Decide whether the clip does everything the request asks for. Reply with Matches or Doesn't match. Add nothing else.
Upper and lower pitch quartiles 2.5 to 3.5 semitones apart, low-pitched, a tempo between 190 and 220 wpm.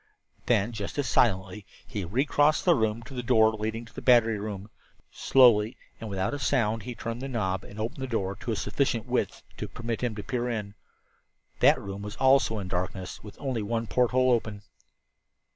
Matches